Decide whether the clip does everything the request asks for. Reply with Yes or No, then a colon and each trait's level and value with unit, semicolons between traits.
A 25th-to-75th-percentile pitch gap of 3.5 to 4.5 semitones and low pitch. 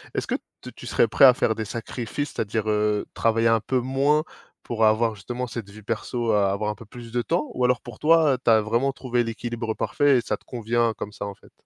No: narrow, 2.6 semitones; low, 115 Hz